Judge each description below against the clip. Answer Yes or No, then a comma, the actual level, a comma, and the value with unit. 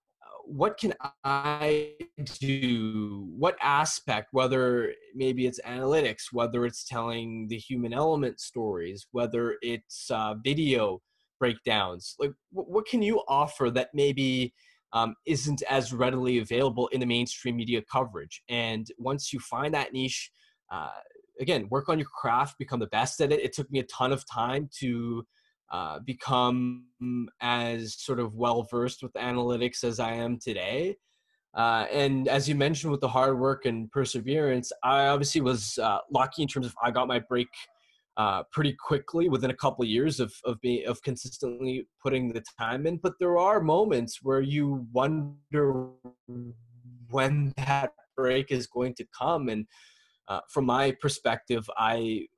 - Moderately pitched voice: No, low, 130 Hz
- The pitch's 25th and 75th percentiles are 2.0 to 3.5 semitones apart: Yes, average, 2.8 semitones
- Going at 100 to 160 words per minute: Yes, average, 155 wpm